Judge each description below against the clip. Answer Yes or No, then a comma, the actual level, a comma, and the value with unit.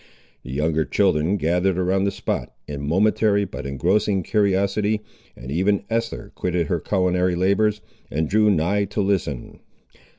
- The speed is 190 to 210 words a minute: No, average, 140 wpm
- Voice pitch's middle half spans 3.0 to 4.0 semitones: Yes, average, 3.6 semitones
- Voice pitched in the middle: No, very low, 95 Hz